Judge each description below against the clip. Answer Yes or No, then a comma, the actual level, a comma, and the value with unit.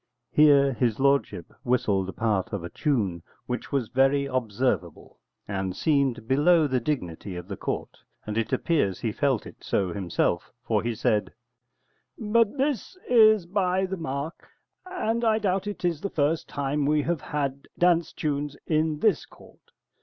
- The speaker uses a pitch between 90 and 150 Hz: Yes, medium, 140 Hz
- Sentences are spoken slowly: No, average, 160 wpm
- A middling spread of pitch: No, wide, 7.3 semitones